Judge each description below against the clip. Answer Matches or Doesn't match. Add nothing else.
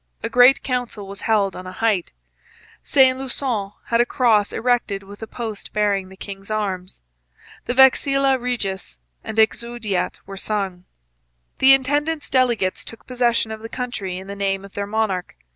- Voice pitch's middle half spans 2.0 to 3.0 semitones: Doesn't match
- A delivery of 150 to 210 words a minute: Matches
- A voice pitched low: Doesn't match